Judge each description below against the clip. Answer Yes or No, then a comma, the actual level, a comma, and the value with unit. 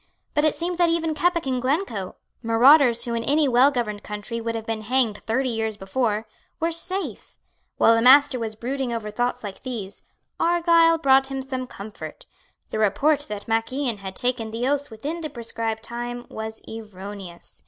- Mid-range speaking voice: No, high, 240 Hz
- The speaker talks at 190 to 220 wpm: No, average, 180 wpm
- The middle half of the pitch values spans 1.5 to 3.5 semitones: No, average, 4.3 semitones